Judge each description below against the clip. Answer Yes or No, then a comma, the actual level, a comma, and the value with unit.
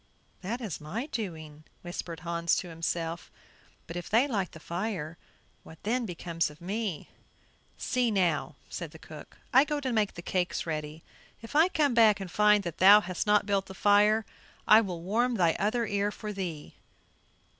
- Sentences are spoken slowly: No, average, 175 wpm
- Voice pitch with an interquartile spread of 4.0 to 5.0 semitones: Yes, average, 4.5 semitones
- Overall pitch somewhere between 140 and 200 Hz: Yes, high, 190 Hz